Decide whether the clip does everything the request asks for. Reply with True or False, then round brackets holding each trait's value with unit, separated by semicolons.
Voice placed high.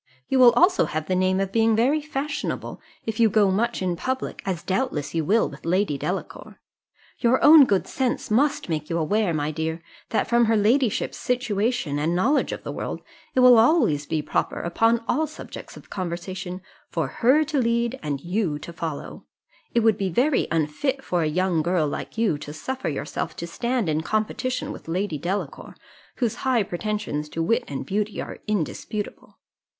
True (205 Hz)